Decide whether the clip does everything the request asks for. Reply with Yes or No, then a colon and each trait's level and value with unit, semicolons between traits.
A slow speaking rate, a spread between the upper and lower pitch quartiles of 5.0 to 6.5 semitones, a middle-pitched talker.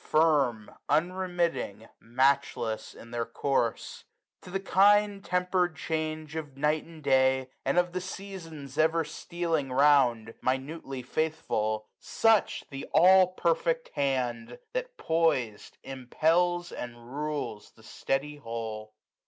Yes: slow, 120 wpm; wide, 5.4 semitones; medium, 150 Hz